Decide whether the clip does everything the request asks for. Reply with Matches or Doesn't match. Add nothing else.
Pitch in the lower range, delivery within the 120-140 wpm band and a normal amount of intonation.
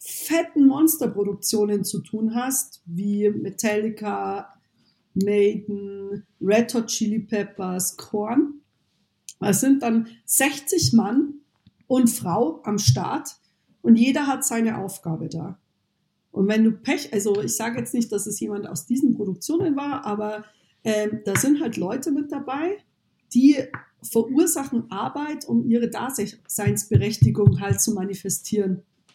Doesn't match